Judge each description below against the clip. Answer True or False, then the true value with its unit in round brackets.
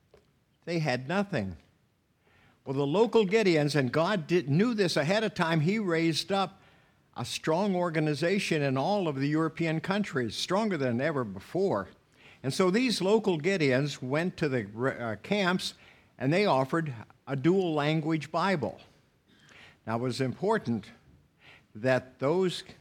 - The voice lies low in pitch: False (160 Hz)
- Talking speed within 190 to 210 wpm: False (140 wpm)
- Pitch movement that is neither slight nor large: False (6.0 semitones)